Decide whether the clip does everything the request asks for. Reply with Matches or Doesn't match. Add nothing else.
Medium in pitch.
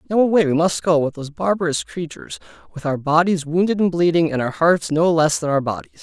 Matches